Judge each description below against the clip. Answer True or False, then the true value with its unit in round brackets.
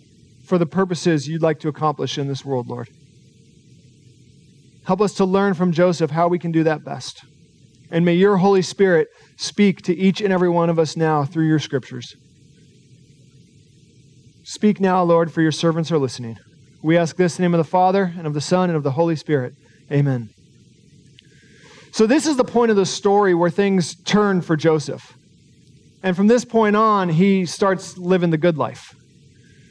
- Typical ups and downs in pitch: True (4.4 semitones)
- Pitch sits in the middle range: True (160 Hz)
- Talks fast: False (185 wpm)